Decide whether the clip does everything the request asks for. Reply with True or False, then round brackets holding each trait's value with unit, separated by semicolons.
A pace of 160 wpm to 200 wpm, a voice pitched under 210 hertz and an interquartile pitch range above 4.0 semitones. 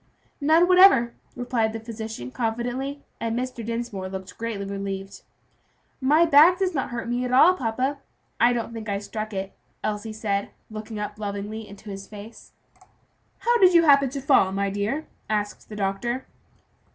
False (165 wpm; 225 Hz; 4.4 semitones)